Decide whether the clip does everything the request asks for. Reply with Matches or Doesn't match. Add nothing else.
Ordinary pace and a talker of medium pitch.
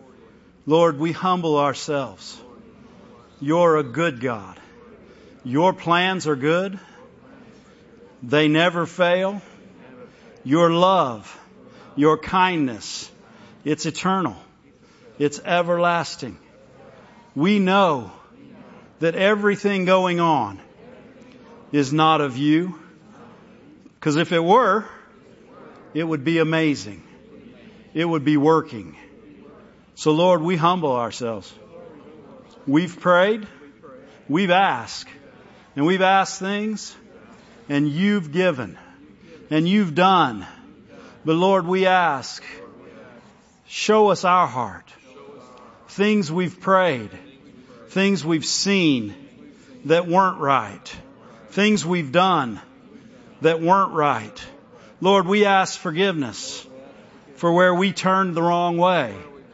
Doesn't match